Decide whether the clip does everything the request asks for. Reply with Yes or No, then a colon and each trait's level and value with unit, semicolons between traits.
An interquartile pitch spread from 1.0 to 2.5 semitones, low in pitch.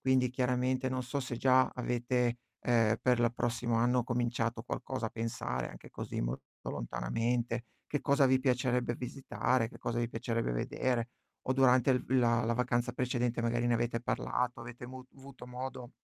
Yes: narrow, 1.5 semitones; low, 125 Hz